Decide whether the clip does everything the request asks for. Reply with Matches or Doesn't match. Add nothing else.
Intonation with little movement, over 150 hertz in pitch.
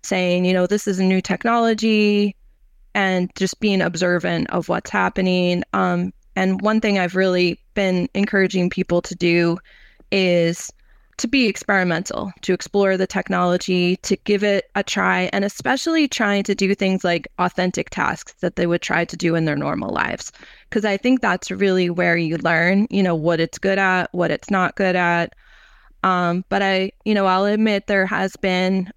Matches